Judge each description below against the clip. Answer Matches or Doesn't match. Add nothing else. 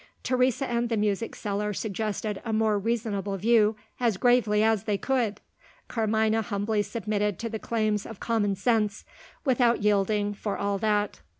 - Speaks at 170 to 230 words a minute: Doesn't match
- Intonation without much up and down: Matches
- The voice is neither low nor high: Doesn't match